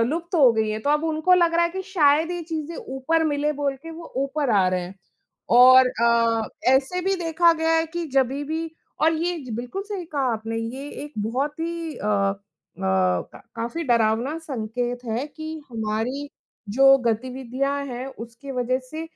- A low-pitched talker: No, very high, 275 Hz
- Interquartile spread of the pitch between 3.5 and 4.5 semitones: No, wide, 5.6 semitones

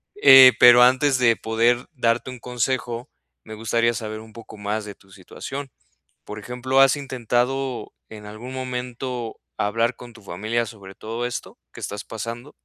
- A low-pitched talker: Yes, low, 120 Hz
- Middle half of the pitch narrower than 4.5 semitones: Yes, narrow, 2.6 semitones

